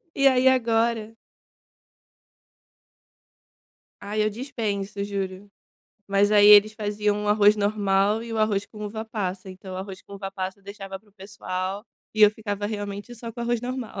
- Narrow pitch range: Yes, narrow, 1.8 semitones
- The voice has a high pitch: Yes, high, 205 Hz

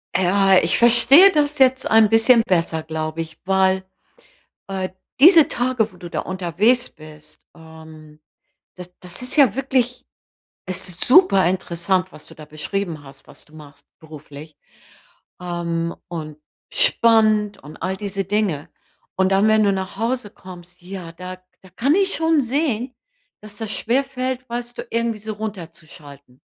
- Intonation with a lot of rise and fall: Yes, wide, 6.0 semitones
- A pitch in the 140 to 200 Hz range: Yes, high, 190 Hz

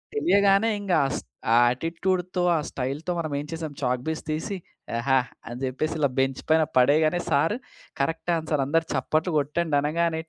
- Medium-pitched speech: Yes, medium, 155 Hz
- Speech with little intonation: No, average, 3.6 semitones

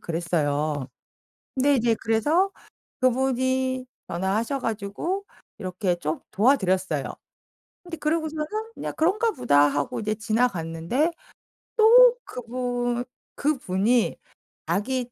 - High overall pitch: Yes, high, 240 Hz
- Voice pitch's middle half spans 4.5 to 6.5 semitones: No, wide, 7.0 semitones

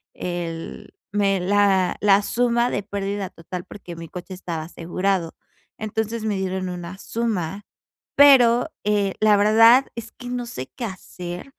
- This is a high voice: Yes, high, 200 Hz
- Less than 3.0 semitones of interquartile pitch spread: No, average, 3.7 semitones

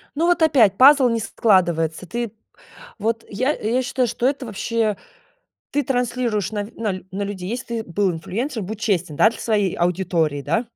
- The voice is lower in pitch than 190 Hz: No, high, 220 Hz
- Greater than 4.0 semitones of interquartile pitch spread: Yes, average, 4.5 semitones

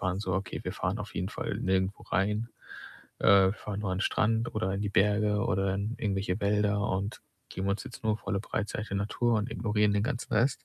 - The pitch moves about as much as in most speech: No, narrow, 1.7 semitones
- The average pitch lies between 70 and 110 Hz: Yes, low, 105 Hz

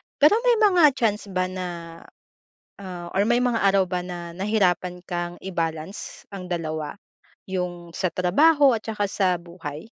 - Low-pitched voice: No, medium, 185 Hz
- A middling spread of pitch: Yes, average, 3.5 semitones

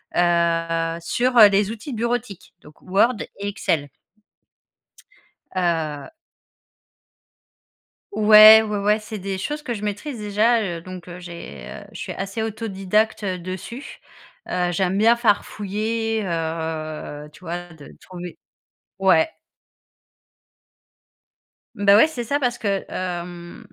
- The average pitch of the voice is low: No, high, 195 Hz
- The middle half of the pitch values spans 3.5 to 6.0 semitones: Yes, average, 4.1 semitones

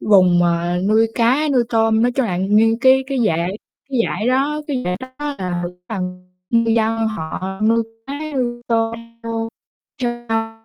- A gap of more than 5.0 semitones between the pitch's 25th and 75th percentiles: No, average, 4.1 semitones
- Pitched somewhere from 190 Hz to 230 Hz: Yes, high, 225 Hz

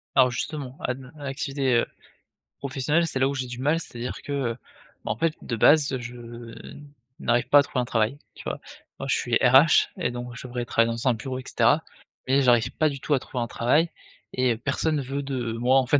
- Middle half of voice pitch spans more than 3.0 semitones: No, narrow, 2.6 semitones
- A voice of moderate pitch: No, low, 130 Hz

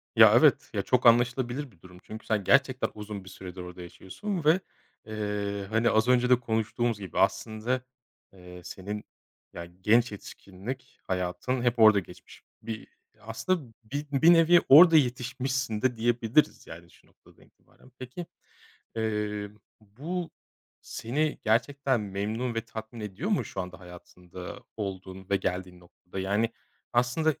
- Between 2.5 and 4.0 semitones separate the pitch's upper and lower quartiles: No, average, 4.6 semitones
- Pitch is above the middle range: No, low, 110 Hz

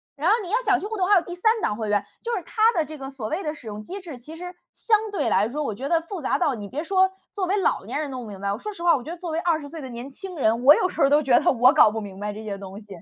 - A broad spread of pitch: Yes, wide, 7.9 semitones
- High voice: Yes, very high, 300 Hz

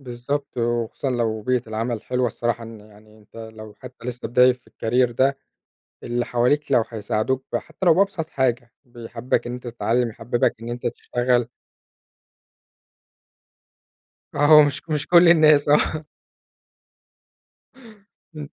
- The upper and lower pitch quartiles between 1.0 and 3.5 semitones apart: Yes, average, 3.0 semitones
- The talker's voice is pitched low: Yes, low, 120 Hz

